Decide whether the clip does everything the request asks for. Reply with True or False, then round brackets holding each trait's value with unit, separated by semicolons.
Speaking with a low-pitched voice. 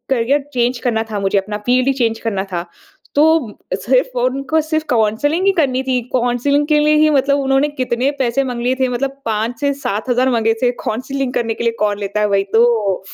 False (250 Hz)